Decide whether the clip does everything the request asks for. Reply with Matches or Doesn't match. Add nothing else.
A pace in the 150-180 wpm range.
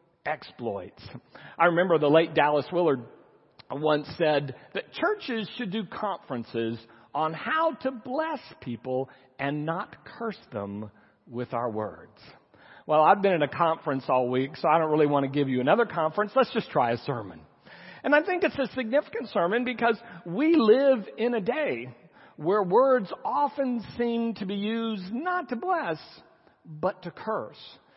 Matches